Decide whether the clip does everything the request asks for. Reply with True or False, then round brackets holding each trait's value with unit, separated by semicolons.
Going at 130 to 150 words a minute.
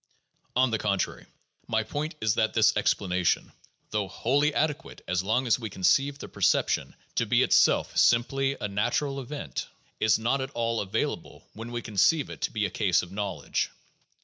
False (175 wpm)